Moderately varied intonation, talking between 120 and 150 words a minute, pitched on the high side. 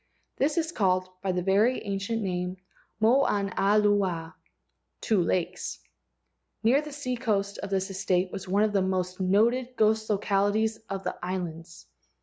Yes: average, 3.0 semitones; slow, 135 wpm; high, 200 Hz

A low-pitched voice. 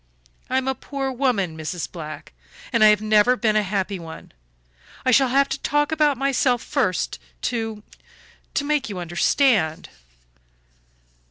No: high, 230 Hz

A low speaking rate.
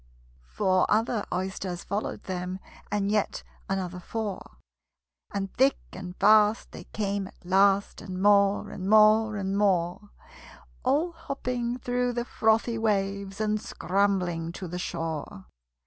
Yes: slow, 130 wpm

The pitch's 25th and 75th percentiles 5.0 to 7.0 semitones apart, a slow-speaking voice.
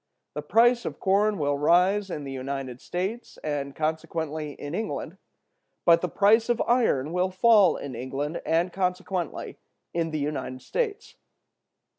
No: wide, 5.5 semitones; average, 145 wpm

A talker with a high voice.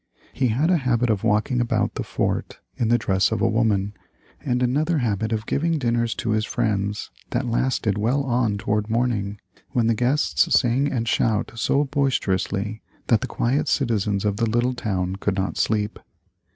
No: low, 115 Hz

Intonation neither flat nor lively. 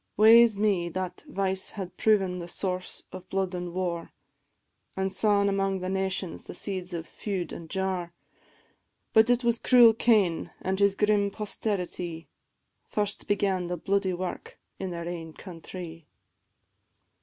No: narrow, 2.3 semitones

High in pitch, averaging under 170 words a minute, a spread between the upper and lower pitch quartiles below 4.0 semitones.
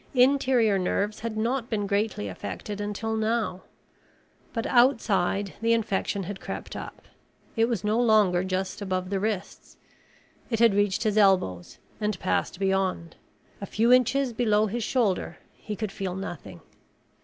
Yes: high, 210 Hz; average, 145 wpm; average, 3.0 semitones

